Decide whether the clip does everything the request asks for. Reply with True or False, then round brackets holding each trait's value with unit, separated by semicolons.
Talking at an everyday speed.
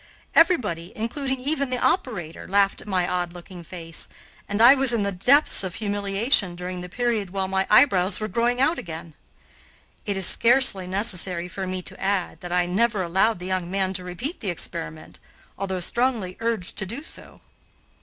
True (180 wpm)